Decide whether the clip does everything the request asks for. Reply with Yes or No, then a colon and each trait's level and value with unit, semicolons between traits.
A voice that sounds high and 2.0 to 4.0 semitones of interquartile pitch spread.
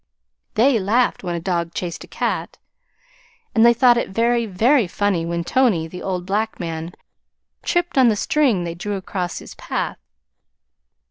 No: high, 200 Hz; average, 5.3 semitones